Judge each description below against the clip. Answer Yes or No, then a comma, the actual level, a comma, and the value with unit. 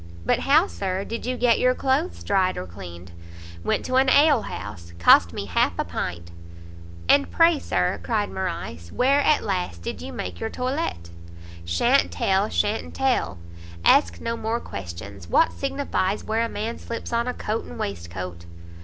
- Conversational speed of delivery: Yes, average, 170 wpm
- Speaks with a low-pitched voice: No, high, 190 Hz